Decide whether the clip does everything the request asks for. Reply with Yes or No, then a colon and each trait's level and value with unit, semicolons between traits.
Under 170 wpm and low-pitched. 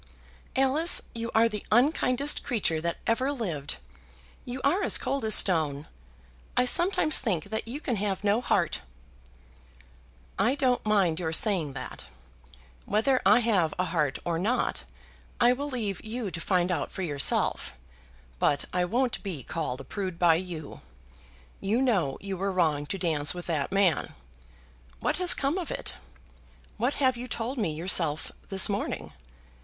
No: average, 160 wpm; high, 200 Hz